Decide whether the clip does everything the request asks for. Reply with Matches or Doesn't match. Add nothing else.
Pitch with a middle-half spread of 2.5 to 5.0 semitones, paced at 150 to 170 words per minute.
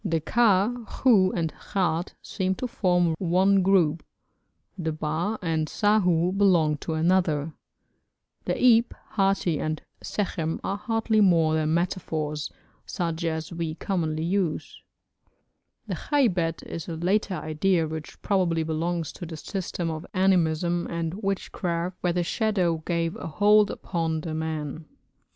Doesn't match